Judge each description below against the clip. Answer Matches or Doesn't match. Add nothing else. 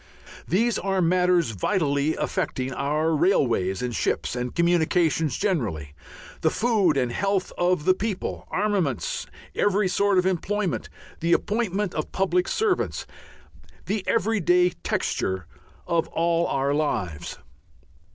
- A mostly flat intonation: Doesn't match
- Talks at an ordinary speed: Doesn't match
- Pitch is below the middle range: Doesn't match